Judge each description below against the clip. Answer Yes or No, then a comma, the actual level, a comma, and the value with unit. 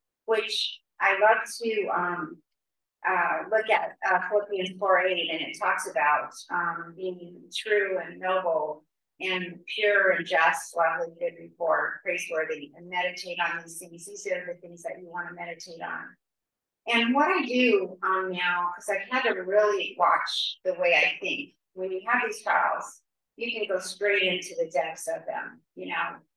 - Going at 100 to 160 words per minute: No, average, 175 wpm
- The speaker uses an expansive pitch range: No, average, 3.2 semitones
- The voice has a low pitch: No, medium, 185 Hz